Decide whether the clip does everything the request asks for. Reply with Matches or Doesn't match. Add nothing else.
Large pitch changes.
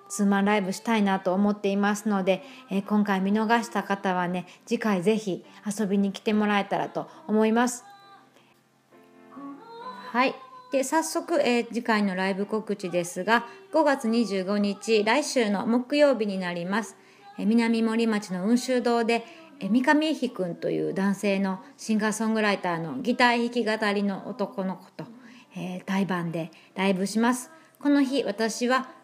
Doesn't match